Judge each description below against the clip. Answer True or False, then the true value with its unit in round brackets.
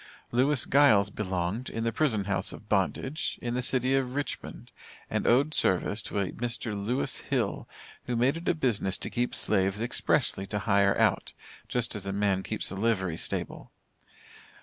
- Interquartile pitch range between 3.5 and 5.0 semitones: True (4.2 semitones)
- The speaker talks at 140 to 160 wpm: False (170 wpm)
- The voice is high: False (110 Hz)